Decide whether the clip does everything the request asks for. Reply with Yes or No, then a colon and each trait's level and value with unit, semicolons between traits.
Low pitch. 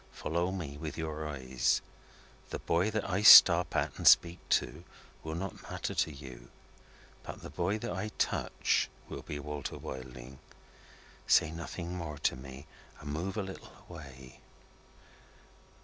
Yes: very low, 80 Hz